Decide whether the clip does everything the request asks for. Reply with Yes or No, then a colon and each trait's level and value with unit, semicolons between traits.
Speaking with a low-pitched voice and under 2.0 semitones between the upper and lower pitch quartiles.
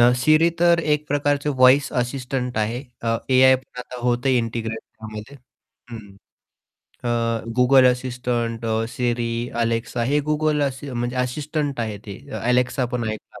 No: low, 125 Hz; average, 2.9 semitones